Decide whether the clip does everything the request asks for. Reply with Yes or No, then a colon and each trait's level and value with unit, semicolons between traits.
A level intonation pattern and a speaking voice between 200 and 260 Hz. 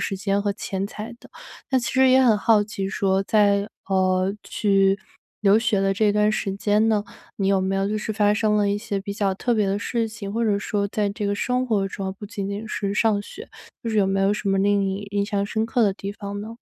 Yes: narrow, 1.6 semitones; high, 205 Hz